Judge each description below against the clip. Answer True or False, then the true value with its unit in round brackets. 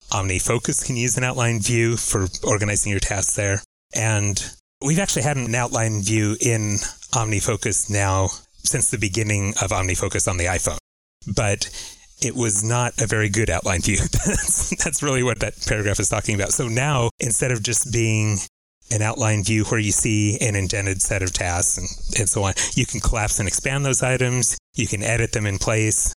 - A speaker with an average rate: True (185 wpm)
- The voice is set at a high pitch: False (110 Hz)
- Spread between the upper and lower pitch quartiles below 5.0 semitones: True (3.2 semitones)